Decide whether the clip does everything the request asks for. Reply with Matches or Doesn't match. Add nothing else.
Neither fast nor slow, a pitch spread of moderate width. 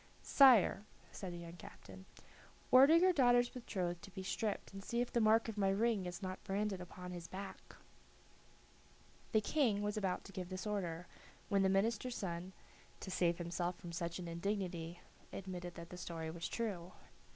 Matches